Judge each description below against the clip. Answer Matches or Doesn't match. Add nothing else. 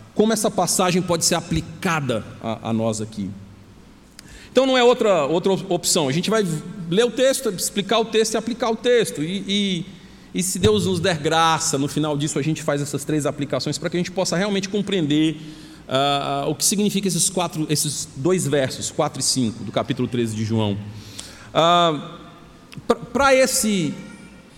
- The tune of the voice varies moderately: Doesn't match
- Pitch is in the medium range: Matches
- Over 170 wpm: Matches